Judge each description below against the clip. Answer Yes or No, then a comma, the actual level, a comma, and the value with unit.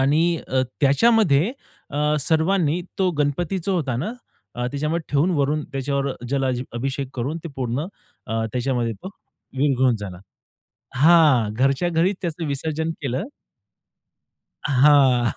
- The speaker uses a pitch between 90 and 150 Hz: Yes, medium, 140 Hz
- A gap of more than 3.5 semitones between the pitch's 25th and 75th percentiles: Yes, average, 3.9 semitones